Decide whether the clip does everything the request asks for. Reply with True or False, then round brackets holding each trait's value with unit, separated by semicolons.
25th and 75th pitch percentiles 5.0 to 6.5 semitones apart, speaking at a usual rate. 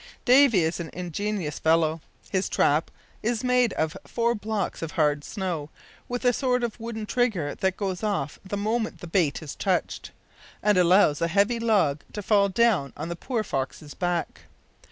True (5.6 semitones; 175 wpm)